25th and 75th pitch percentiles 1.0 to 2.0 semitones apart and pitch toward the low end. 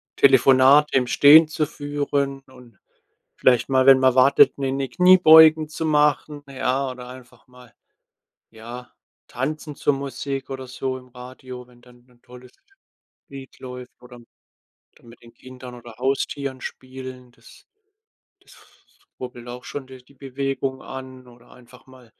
Yes: narrow, 1.7 semitones; low, 130 Hz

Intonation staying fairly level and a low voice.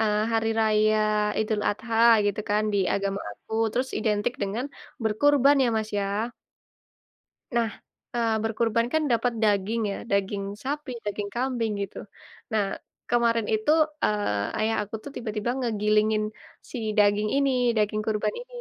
No: narrow, 2.1 semitones; high, 215 Hz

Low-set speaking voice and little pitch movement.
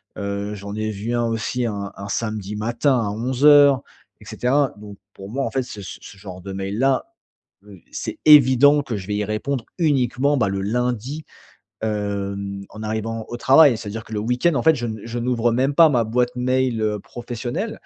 No: low, 115 Hz; average, 3.9 semitones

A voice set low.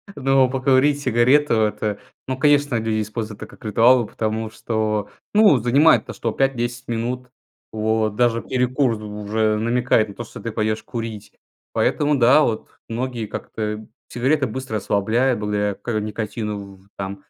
Yes: low, 115 Hz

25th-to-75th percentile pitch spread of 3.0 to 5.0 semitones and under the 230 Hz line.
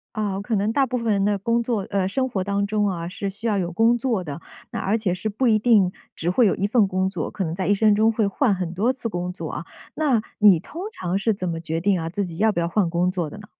Yes: average, 3.4 semitones; high, 200 Hz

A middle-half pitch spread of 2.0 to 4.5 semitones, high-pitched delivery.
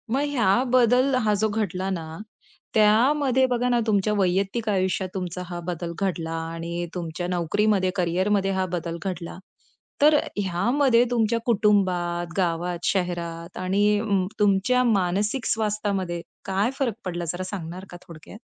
Yes: average, 3.6 semitones; high, 195 Hz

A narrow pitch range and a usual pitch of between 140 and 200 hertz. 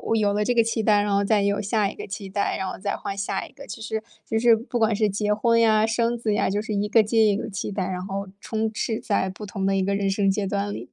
No: narrow, 1.9 semitones; high, 210 Hz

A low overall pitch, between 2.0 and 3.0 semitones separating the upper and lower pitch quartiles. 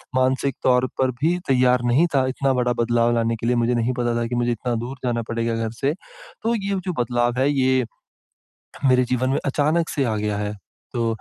Yes: low, 125 Hz; narrow, 2.5 semitones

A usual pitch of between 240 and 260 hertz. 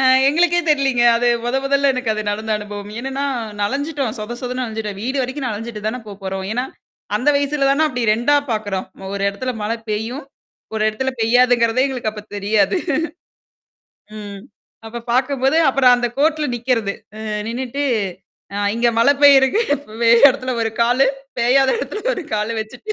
Yes: high, 245 Hz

